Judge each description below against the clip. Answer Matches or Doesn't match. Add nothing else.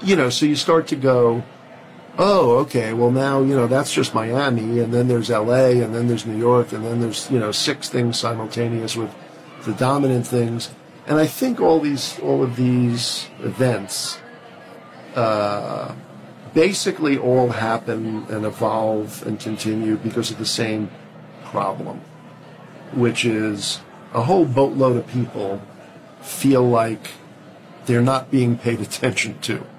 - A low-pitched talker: Matches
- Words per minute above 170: Doesn't match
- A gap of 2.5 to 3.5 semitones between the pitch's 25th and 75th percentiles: Matches